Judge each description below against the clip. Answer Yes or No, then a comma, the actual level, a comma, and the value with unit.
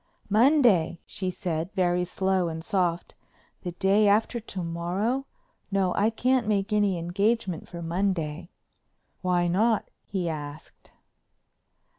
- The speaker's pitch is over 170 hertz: Yes, medium, 185 Hz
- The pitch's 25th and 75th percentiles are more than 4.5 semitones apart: No, average, 3.4 semitones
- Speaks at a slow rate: Yes, slow, 120 wpm